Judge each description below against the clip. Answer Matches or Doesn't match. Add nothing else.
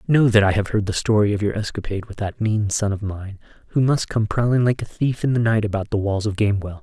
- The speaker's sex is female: Doesn't match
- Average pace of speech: Doesn't match